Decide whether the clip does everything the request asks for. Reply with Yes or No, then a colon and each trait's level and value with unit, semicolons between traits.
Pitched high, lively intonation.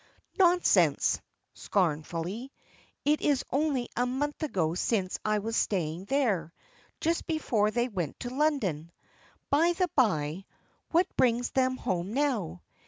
Yes: high, 240 Hz; wide, 7.8 semitones